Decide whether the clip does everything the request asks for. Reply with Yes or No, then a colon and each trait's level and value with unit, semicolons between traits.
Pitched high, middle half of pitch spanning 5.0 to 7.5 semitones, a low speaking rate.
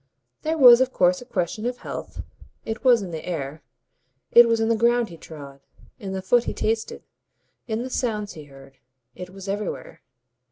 No: high, 210 Hz; wide, 5.4 semitones; average, 190 wpm